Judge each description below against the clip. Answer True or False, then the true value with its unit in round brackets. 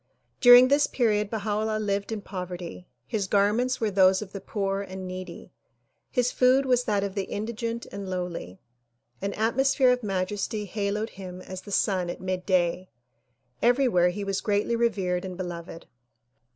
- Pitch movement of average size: True (3.3 semitones)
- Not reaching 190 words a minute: True (160 wpm)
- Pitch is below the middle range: False (200 Hz)